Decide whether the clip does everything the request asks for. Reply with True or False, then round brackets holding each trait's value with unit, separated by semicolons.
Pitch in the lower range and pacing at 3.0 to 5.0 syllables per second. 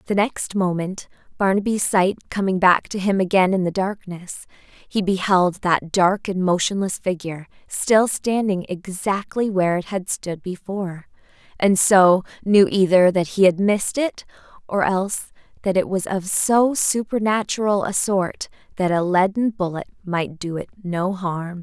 False (190 Hz; 4.4 syllables/s)